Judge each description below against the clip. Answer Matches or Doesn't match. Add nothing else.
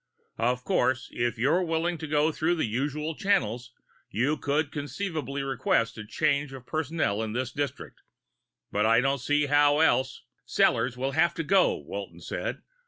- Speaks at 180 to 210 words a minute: Doesn't match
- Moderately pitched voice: Matches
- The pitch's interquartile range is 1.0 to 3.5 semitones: Doesn't match